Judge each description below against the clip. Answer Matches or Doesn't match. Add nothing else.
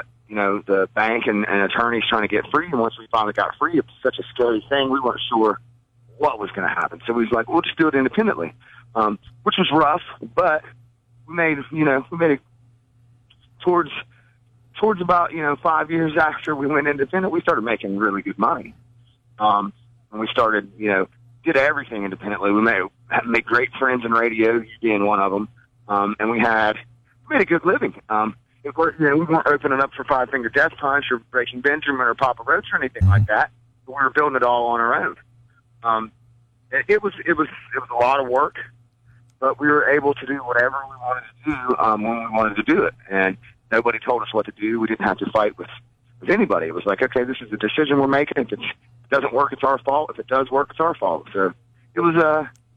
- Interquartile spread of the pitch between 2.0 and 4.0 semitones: Matches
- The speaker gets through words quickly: Matches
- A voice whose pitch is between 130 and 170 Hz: Doesn't match